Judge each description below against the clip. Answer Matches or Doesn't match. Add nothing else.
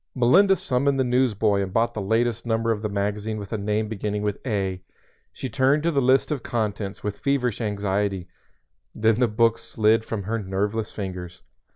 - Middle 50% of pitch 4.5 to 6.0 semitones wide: Doesn't match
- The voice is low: Matches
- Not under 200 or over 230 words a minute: Doesn't match